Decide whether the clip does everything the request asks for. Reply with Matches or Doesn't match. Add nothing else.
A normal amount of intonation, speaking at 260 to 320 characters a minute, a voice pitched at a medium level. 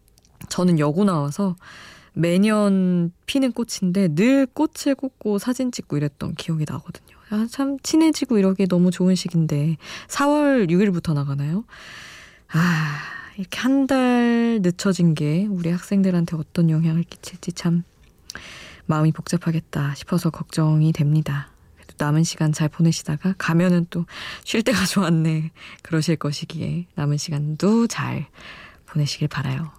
Matches